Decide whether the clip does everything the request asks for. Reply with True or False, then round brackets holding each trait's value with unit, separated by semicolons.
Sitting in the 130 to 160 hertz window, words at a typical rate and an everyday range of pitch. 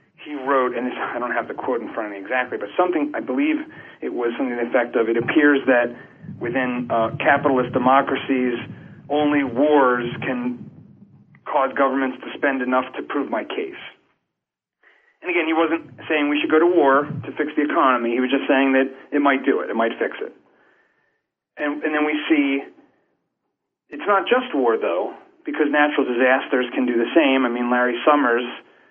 True (140 Hz; 190 wpm; 3.3 semitones)